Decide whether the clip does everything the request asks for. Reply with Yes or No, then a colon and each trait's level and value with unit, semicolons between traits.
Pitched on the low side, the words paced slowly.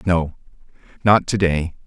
Yes: very low, 90 Hz; slow, 130 wpm